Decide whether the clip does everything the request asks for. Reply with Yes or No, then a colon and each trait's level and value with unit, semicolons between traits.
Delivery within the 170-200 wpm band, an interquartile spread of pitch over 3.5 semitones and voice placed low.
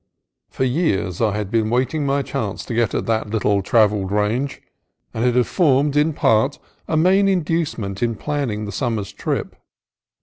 Yes: average, 175 wpm; wide, 5.4 semitones; low, 120 Hz